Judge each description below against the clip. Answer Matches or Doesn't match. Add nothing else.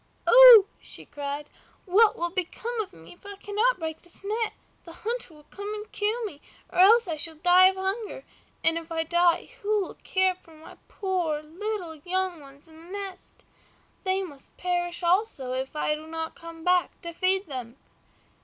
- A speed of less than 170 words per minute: Doesn't match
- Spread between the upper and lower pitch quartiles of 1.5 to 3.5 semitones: Doesn't match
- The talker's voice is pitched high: Matches